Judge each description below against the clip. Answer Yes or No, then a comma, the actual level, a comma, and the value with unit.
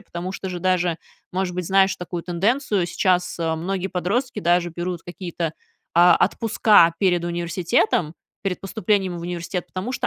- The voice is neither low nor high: Yes, medium, 180 Hz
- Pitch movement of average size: No, narrow, 1.8 semitones